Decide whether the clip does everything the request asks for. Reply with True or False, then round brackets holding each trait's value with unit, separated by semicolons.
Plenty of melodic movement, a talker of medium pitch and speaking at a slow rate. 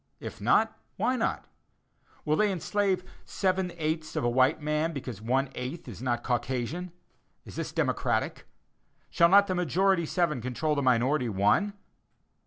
False (6.2 semitones; 155 Hz; 150 wpm)